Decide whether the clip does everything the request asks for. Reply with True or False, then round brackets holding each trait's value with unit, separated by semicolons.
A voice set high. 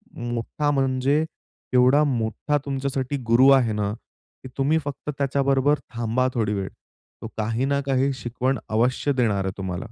False (130 Hz)